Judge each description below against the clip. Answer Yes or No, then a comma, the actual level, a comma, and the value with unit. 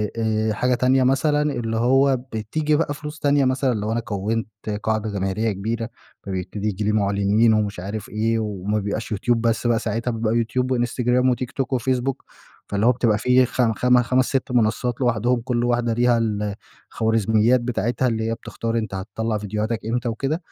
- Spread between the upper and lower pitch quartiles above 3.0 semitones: No, average, 2.7 semitones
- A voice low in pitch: Yes, low, 115 Hz